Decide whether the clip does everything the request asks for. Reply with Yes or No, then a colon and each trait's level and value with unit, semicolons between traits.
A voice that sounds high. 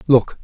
No: low, 130 Hz